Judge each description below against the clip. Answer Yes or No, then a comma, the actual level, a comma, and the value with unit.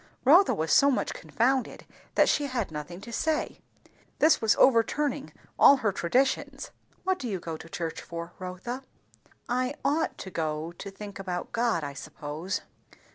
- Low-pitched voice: No, high, 205 Hz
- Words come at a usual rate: Yes, average, 160 wpm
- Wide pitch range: Yes, wide, 7.7 semitones